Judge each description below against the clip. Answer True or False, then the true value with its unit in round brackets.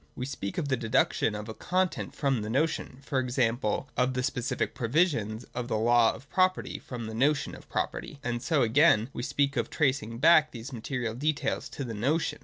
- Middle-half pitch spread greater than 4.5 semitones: False (3.8 semitones)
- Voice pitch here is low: True (125 Hz)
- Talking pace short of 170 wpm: False (195 wpm)